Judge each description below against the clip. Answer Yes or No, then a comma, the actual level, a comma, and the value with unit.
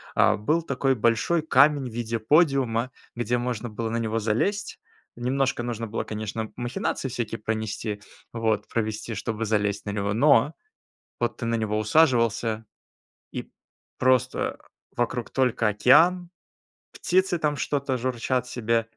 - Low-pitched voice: Yes, low, 120 Hz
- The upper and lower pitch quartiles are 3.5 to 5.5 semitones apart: No, average, 3.1 semitones